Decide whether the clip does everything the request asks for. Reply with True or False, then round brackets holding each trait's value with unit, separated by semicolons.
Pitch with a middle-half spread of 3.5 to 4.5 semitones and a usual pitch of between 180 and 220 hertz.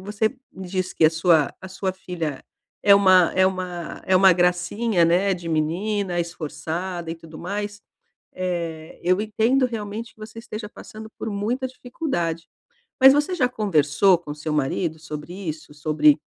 True (4.1 semitones; 185 Hz)